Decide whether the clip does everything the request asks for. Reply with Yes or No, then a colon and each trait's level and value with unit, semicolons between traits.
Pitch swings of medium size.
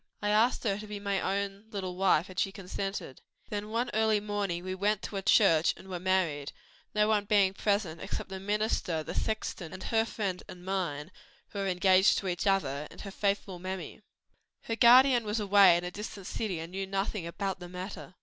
No: narrow, 2.3 semitones